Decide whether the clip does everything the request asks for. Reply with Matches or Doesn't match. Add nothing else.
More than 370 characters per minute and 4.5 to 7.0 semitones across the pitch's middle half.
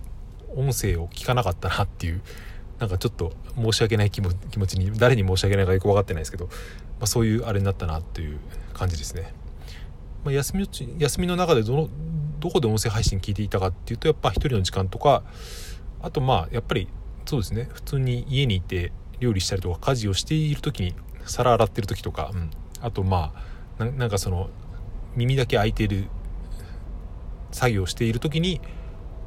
Matches